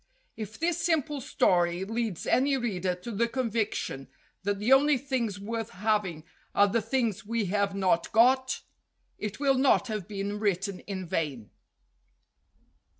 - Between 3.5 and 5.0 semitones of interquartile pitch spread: Yes, average, 4.1 semitones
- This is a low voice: No, high, 215 Hz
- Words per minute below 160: Yes, average, 150 wpm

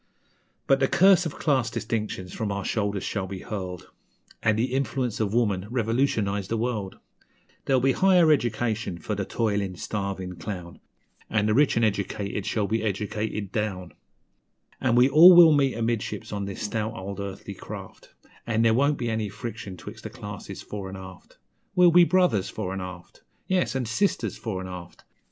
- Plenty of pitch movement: No, average, 4.0 semitones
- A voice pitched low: Yes, low, 110 Hz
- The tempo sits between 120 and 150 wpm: No, average, 175 wpm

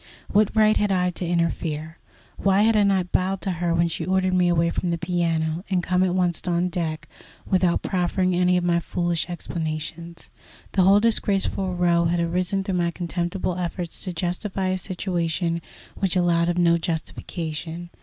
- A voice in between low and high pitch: Yes, medium, 175 Hz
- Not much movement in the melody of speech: Yes, narrow, 1.7 semitones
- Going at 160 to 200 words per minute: Yes, average, 175 wpm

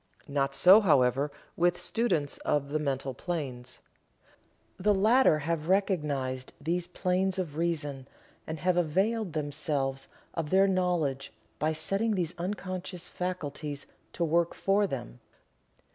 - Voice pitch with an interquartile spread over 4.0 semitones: Yes, average, 4.5 semitones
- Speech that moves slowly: Yes, slow, 125 wpm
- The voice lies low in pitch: No, medium, 165 Hz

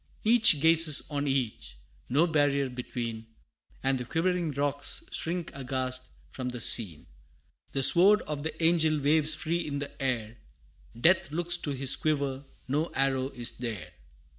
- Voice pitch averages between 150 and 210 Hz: No, medium, 140 Hz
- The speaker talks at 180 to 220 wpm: No, average, 145 wpm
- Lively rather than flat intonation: No, average, 3.8 semitones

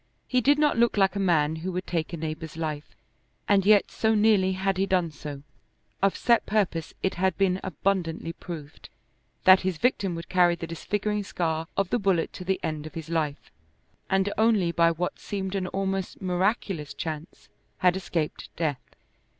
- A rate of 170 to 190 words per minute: Yes, average, 180 wpm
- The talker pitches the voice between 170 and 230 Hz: Yes, medium, 185 Hz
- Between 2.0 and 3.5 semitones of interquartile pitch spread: Yes, average, 3.2 semitones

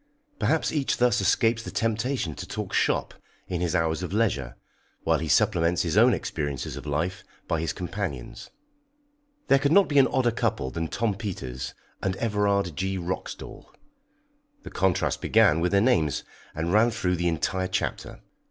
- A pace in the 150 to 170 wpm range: Yes, average, 165 wpm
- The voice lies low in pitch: Yes, very low, 95 Hz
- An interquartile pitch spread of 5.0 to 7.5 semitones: Yes, wide, 5.4 semitones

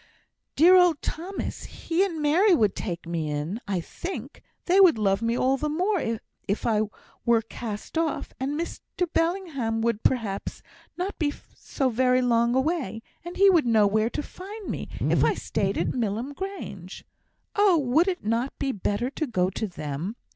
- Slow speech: No, average, 175 wpm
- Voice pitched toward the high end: Yes, very high, 255 Hz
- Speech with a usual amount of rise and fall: No, wide, 7.9 semitones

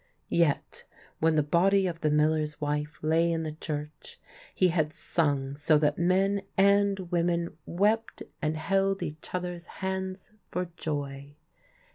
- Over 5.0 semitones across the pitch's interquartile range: No, average, 3.8 semitones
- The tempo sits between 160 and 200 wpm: No, average, 140 wpm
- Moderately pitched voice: Yes, medium, 165 Hz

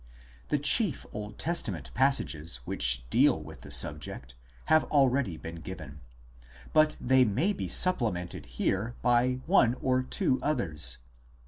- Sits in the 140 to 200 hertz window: No, low, 120 Hz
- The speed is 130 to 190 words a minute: Yes, average, 140 wpm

